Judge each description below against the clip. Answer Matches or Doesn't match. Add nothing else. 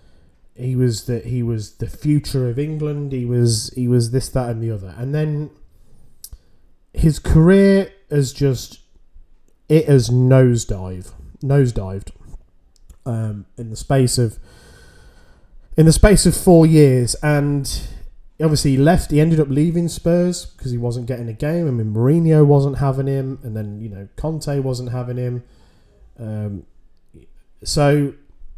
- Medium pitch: Doesn't match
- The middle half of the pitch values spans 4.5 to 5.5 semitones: Matches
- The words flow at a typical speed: Matches